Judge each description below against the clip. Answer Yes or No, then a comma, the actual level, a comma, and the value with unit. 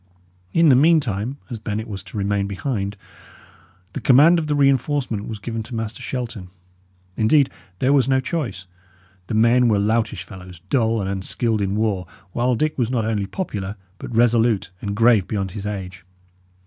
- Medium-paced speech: Yes, average, 170 wpm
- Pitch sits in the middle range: No, low, 110 Hz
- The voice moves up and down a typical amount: Yes, average, 4.1 semitones